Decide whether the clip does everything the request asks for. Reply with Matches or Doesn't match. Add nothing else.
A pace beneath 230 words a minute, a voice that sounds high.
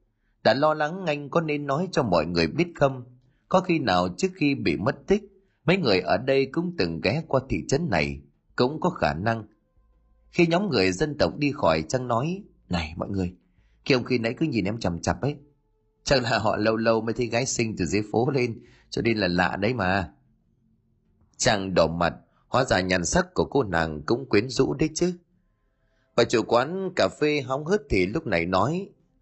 Doesn't match